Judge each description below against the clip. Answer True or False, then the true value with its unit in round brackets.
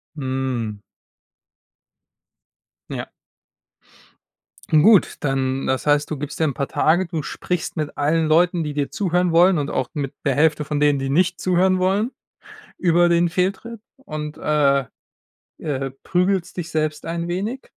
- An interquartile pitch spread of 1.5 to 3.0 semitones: False (3.6 semitones)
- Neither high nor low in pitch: True (155 Hz)